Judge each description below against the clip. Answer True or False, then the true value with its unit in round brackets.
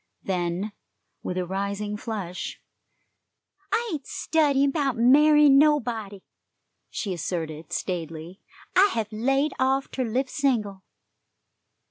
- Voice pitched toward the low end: False (225 Hz)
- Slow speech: True (105 wpm)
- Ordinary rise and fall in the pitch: False (6.5 semitones)